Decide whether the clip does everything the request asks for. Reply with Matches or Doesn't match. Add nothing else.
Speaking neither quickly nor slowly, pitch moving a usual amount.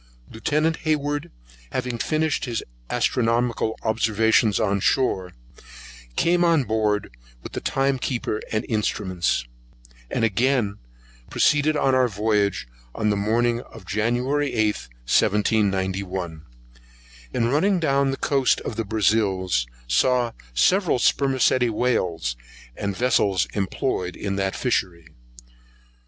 Doesn't match